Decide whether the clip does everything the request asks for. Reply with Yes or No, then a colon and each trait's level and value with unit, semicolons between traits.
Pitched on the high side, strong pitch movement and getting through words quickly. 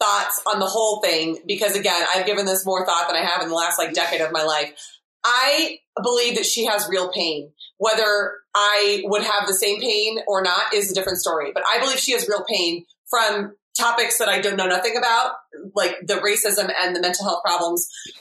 No: high, 200 Hz; average, 3.7 semitones; fast, 215 wpm